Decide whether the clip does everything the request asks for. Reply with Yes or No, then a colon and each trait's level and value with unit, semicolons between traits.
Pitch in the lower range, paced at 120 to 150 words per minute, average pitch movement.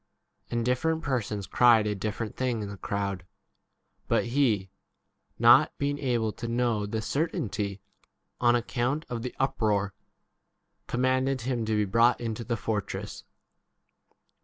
Yes: low, 115 Hz; slow, 135 wpm; average, 3.2 semitones